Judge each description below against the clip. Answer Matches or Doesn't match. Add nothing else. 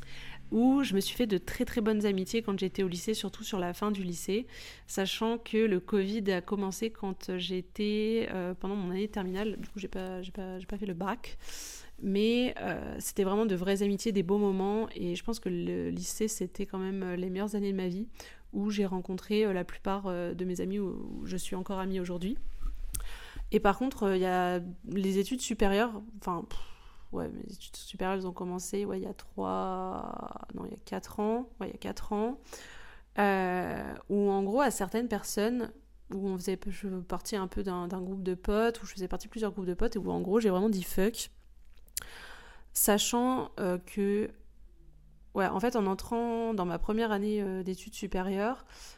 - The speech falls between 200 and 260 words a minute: Matches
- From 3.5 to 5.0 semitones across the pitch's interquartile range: Doesn't match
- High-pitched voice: Matches